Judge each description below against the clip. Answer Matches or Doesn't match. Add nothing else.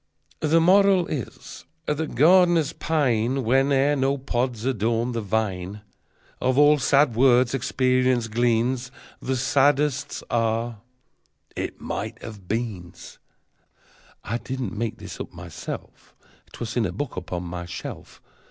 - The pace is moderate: Doesn't match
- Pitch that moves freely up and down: Doesn't match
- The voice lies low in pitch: Matches